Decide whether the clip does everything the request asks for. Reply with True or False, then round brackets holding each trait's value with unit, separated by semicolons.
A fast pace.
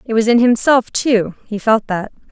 True (210 wpm)